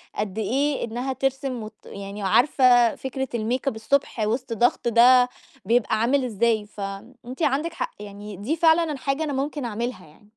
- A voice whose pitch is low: No, high, 245 Hz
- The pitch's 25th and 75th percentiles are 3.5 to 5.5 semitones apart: Yes, average, 4.0 semitones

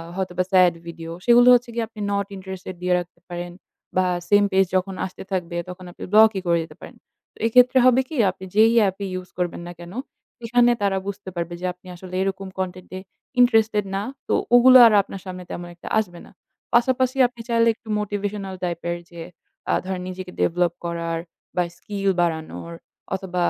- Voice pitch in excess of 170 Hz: Yes, high, 190 Hz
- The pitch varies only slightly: No, average, 3.6 semitones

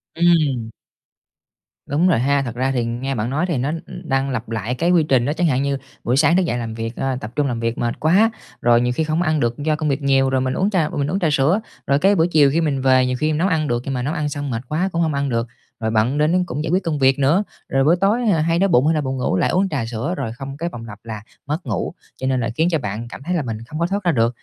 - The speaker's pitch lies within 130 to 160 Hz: Yes, medium, 140 Hz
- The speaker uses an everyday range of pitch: Yes, average, 4.8 semitones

